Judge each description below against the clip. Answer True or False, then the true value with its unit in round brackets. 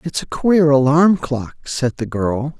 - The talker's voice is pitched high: False (145 Hz)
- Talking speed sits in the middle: True (185 wpm)